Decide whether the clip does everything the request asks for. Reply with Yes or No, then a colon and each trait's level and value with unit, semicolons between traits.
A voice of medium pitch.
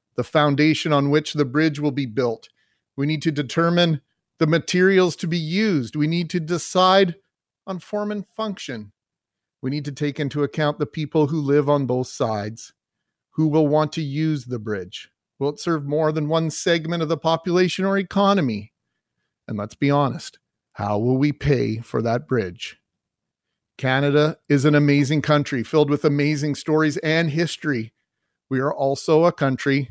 Yes: medium, 150 Hz